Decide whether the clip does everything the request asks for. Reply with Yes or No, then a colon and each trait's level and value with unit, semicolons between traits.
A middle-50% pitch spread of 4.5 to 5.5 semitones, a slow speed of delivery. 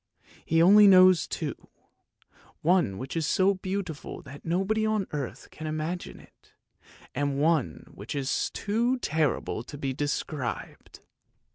Yes: average, 4.9 semitones; slow, 130 wpm